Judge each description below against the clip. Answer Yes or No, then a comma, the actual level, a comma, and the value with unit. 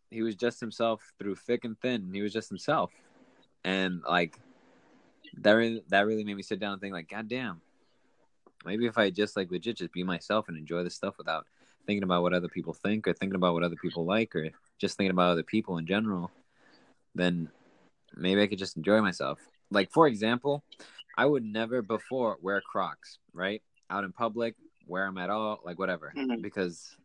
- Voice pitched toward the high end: No, low, 100 Hz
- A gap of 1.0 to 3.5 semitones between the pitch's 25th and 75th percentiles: No, average, 3.9 semitones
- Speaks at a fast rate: No, average, 195 wpm